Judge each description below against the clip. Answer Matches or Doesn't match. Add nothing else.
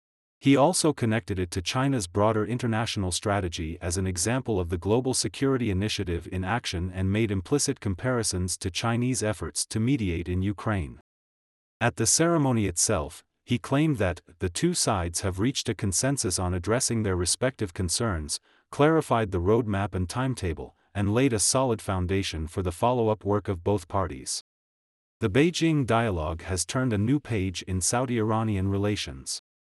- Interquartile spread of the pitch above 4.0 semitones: Matches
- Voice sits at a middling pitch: Doesn't match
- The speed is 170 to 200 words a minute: Doesn't match